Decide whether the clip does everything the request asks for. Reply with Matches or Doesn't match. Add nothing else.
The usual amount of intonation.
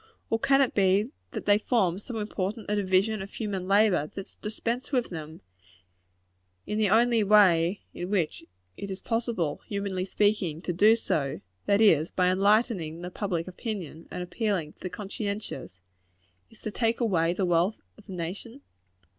Matches